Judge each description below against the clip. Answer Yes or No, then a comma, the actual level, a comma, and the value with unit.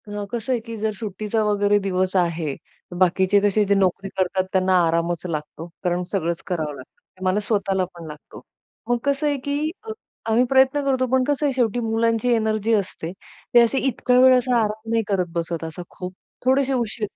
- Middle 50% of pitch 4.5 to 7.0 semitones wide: Yes, average, 4.9 semitones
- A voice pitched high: Yes, high, 210 Hz